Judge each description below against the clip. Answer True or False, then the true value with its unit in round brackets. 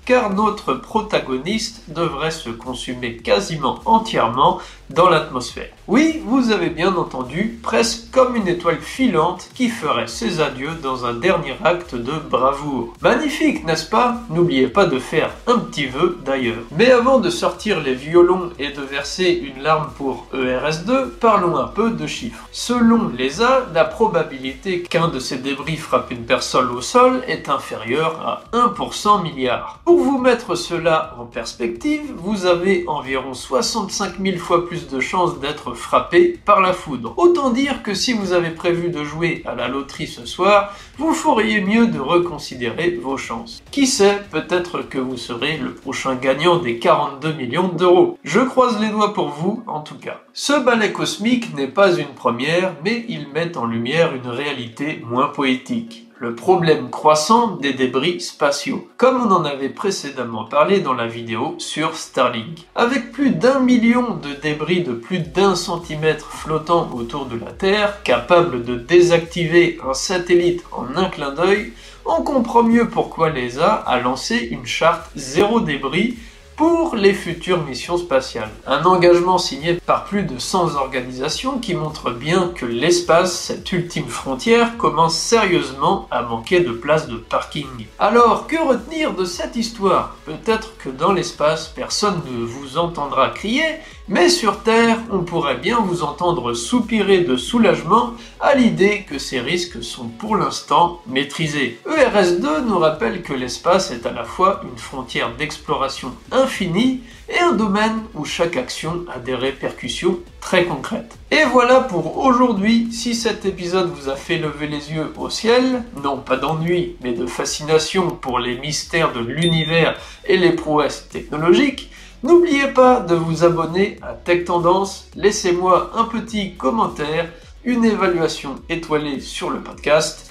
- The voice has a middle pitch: True (175 Hz)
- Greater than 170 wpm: False (160 wpm)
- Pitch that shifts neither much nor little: False (7.2 semitones)